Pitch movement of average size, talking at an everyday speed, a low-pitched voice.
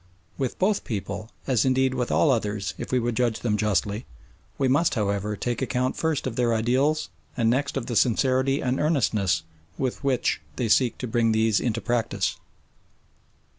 Yes: average, 3.2 semitones; average, 170 wpm; low, 120 Hz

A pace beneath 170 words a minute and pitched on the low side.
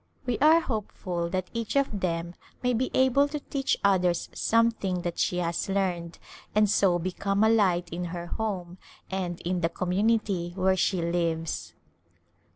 No: average, 160 wpm; medium, 185 Hz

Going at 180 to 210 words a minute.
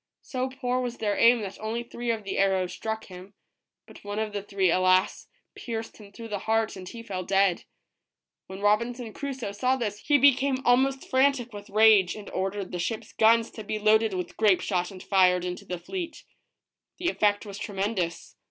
Yes: average, 190 wpm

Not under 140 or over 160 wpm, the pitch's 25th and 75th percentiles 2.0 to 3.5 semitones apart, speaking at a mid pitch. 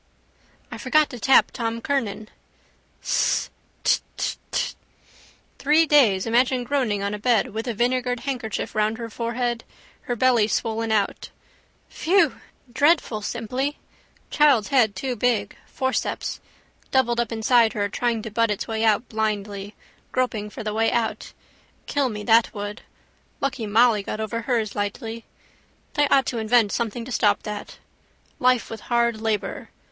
No: average, 150 wpm; average, 2.8 semitones; high, 230 Hz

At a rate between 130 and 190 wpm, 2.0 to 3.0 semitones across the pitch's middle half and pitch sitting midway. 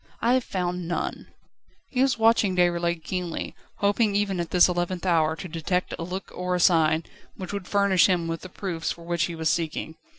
No: average, 200 wpm; narrow, 2.5 semitones; medium, 180 Hz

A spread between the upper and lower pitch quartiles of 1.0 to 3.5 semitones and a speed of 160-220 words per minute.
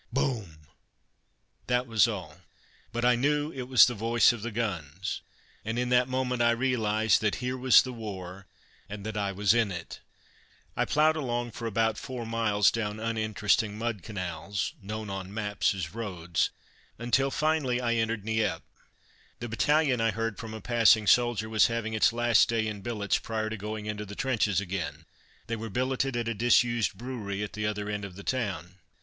Yes: average, 2.7 semitones; average, 180 wpm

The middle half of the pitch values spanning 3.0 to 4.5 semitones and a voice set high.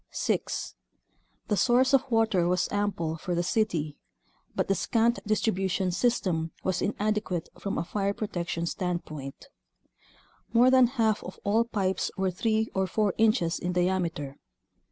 Yes: average, 4.0 semitones; high, 195 Hz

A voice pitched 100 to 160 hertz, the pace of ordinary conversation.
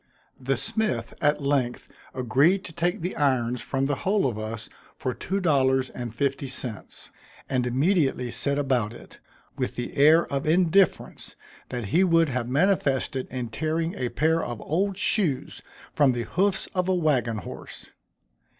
Yes: medium, 140 Hz; average, 160 wpm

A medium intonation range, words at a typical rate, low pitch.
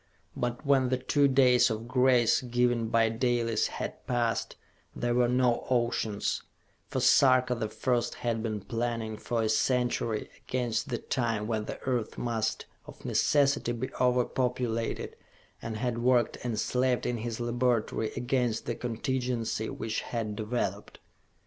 No: narrow, 1.8 semitones; average, 145 wpm; low, 120 Hz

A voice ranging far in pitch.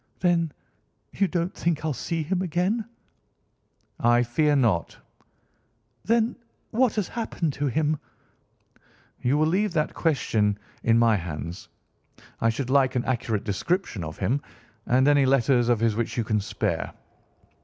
Yes: wide, 6.7 semitones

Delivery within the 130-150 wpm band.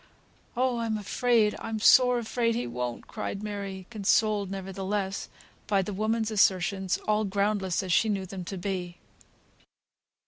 Yes: average, 140 wpm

